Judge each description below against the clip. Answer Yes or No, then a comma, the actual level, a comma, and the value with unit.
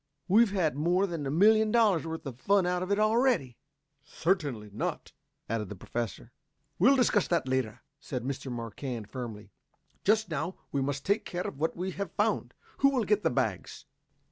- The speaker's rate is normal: Yes, average, 180 wpm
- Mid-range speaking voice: Yes, medium, 165 Hz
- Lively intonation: Yes, wide, 7.8 semitones